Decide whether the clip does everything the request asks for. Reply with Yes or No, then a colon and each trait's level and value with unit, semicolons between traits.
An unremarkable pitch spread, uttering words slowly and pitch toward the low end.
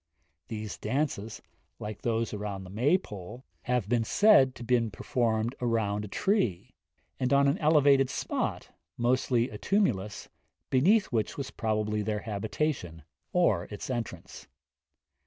Yes: average, 4.3 semitones; slow, 130 wpm; low, 115 Hz